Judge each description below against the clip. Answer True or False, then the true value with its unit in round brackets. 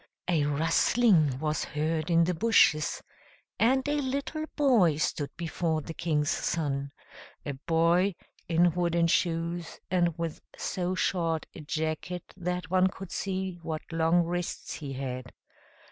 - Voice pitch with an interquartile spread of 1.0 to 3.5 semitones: True (2.5 semitones)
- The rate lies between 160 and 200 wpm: False (135 wpm)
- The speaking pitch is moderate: True (170 Hz)